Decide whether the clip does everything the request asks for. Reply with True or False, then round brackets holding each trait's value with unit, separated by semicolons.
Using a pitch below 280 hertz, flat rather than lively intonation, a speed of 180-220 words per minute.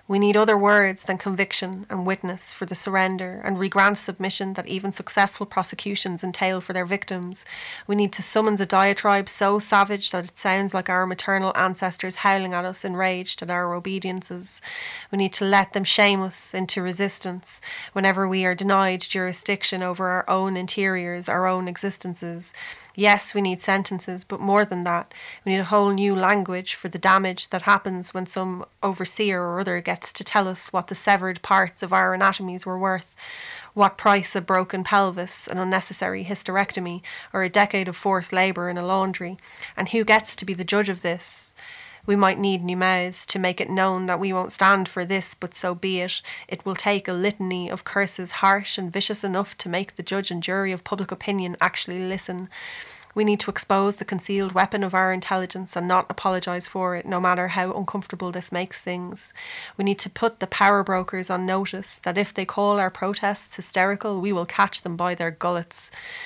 True (190 Hz; 1.4 semitones; 195 wpm)